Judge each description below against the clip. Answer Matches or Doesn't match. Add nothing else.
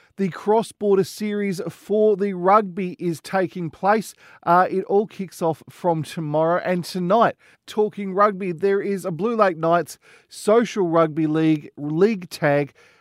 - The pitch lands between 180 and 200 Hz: Matches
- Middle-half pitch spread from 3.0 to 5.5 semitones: Matches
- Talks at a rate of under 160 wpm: Matches